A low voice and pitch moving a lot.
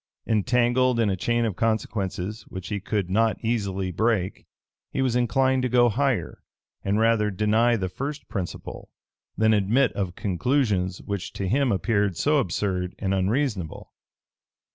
No: low, 110 Hz; average, 4.0 semitones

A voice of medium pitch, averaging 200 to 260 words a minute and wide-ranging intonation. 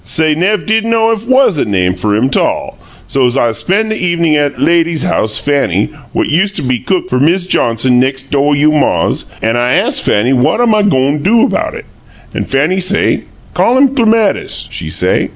Yes: medium, 155 Hz; fast, 205 wpm; wide, 8.1 semitones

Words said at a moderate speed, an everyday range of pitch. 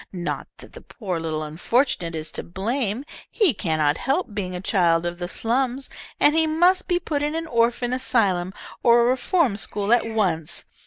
No: average, 180 wpm; wide, 7.4 semitones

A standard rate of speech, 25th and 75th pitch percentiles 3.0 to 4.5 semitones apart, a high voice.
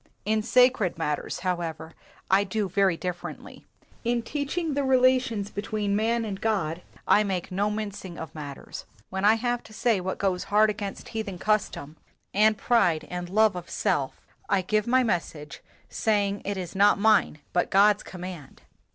Yes: average, 160 wpm; average, 3.4 semitones; high, 200 Hz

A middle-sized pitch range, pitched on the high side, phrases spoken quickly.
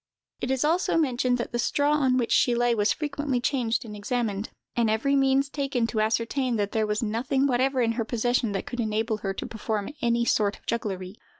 Yes: average, 3.4 semitones; high, 240 Hz; fast, 210 wpm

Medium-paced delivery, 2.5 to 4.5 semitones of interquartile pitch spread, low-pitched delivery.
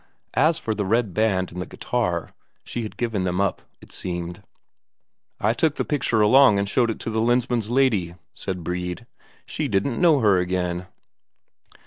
No: average, 170 wpm; average, 4.9 semitones; low, 105 Hz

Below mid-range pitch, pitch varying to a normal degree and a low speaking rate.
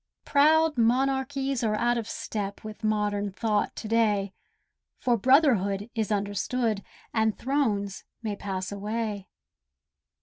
No: high, 220 Hz; average, 3.7 semitones; slow, 115 wpm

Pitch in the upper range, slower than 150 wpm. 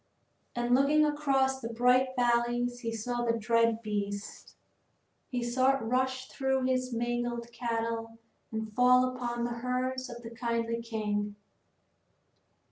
Yes: high, 240 Hz; slow, 135 wpm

